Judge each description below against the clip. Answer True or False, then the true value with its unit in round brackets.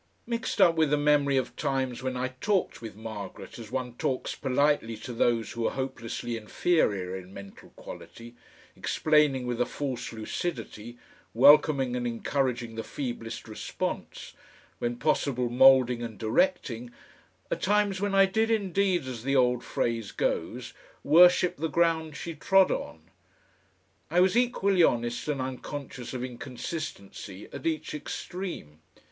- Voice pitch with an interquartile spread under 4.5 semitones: False (5.3 semitones)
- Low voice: True (130 Hz)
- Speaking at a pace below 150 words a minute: True (140 wpm)